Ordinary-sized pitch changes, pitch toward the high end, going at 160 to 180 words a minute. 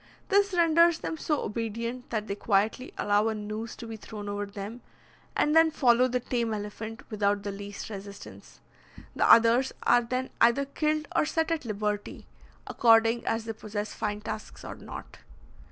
Yes: average, 3.5 semitones; high, 225 Hz; average, 170 wpm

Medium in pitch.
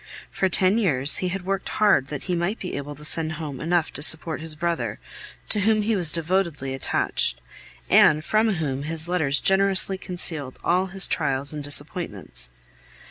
Yes: medium, 165 Hz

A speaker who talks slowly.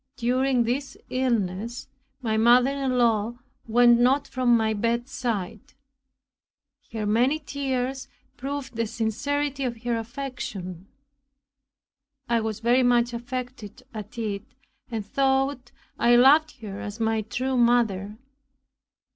Yes: slow, 115 wpm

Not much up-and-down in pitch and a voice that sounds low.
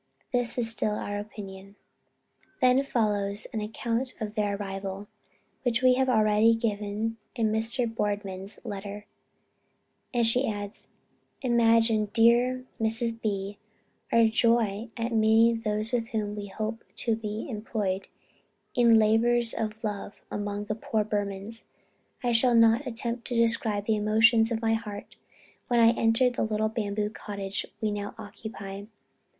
No: narrow, 2.0 semitones; high, 220 Hz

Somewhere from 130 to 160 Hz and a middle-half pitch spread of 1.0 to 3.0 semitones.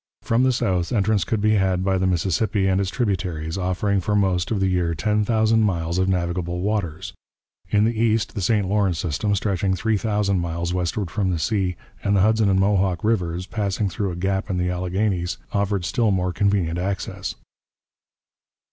No: very low, 95 Hz; average, 2.7 semitones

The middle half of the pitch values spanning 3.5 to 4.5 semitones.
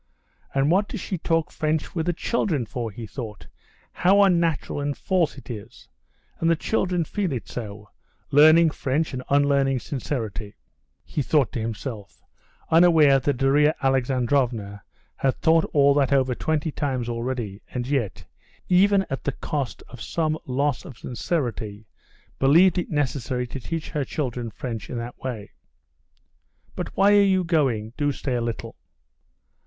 No: average, 4.9 semitones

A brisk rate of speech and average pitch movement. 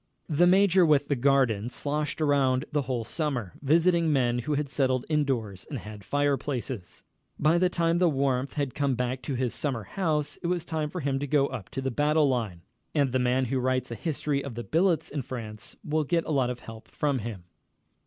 Yes: fast, 210 wpm; average, 3.4 semitones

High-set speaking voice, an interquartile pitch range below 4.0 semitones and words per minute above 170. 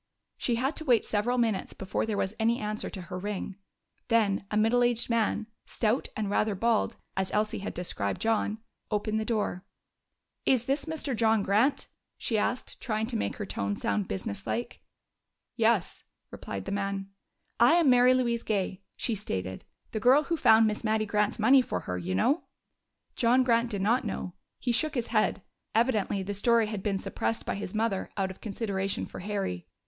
Yes: high, 215 Hz; average, 3.2 semitones; average, 185 wpm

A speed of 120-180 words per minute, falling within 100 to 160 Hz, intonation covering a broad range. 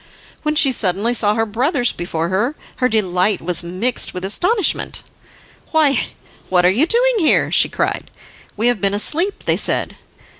No: average, 160 wpm; high, 225 Hz; wide, 8.0 semitones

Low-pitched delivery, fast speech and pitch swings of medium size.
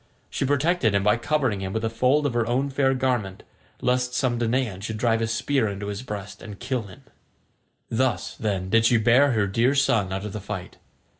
Yes: low, 115 Hz; fast, 210 wpm; average, 4.1 semitones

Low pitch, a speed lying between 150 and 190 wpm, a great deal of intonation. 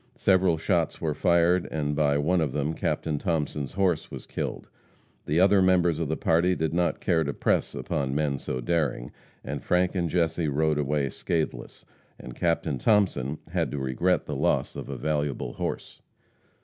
No: very low, 80 Hz; average, 175 wpm; average, 3.2 semitones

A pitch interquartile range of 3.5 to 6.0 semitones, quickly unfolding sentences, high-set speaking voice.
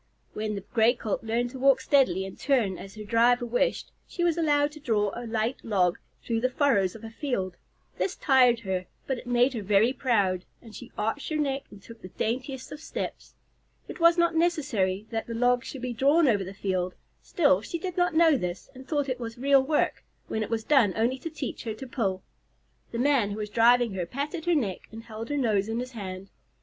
Yes: average, 4.7 semitones; fast, 225 wpm; high, 240 Hz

